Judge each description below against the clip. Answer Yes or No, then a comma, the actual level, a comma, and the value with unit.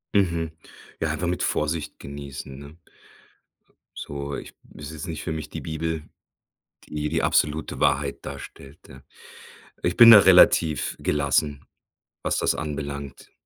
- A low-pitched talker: Yes, very low, 75 Hz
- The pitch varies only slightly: Yes, narrow, 2.3 semitones